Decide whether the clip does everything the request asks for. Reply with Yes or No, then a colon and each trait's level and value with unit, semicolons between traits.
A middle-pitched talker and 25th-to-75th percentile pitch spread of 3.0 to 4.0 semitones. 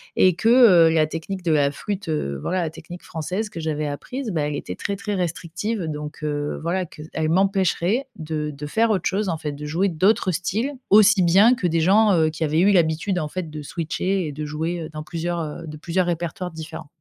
Yes: medium, 170 Hz; average, 3.6 semitones